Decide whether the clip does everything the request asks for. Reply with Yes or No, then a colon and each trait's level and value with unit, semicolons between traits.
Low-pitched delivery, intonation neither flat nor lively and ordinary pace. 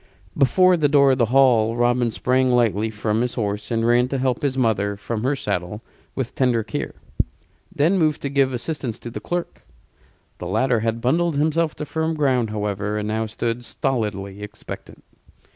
Yes: low, 120 Hz; average, 4.1 semitones; average, 175 wpm